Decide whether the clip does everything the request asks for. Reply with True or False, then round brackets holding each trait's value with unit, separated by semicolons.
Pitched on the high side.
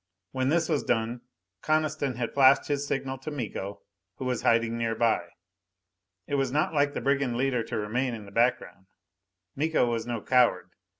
False (125 Hz)